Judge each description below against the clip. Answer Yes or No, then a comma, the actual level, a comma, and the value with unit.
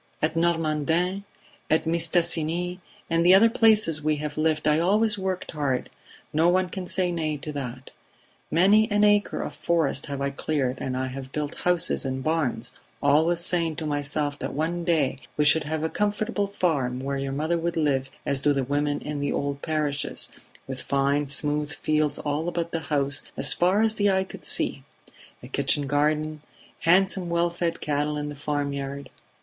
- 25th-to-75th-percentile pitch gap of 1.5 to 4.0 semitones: Yes, average, 3.3 semitones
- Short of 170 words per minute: No, average, 180 wpm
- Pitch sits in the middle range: Yes, medium, 155 Hz